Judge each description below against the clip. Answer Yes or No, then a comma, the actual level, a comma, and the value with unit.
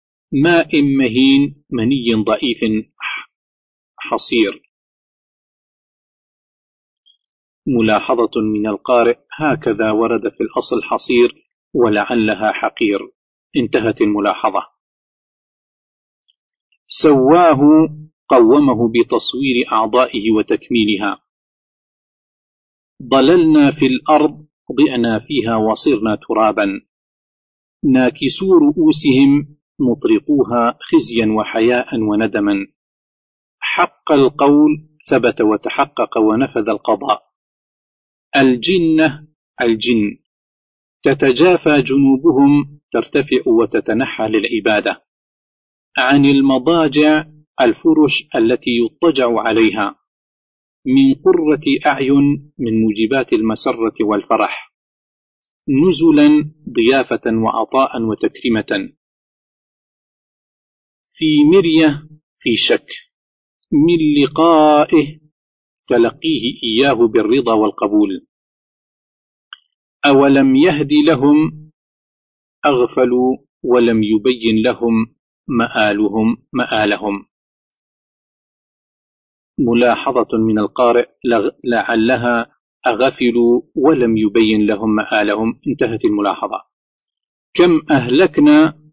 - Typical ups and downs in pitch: No, wide, 5.9 semitones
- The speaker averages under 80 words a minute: Yes, slow, 65 wpm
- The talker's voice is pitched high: No, medium, 140 Hz